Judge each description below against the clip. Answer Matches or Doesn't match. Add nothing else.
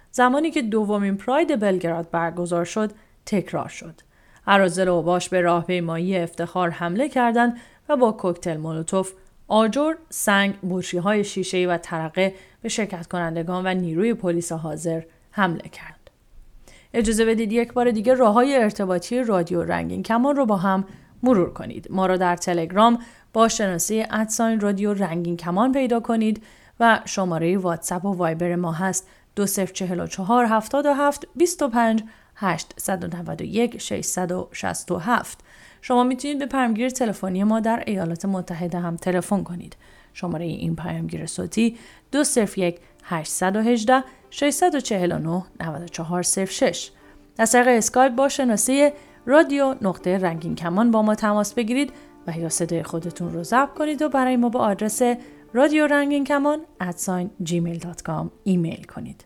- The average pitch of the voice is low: Doesn't match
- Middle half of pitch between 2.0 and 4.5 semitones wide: Doesn't match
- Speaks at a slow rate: Matches